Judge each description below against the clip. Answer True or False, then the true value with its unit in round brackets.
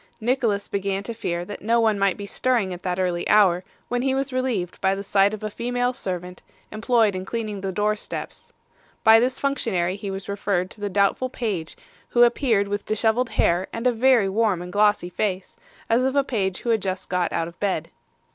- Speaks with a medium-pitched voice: False (205 Hz)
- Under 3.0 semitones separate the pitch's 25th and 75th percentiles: False (3.7 semitones)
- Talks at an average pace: False (210 wpm)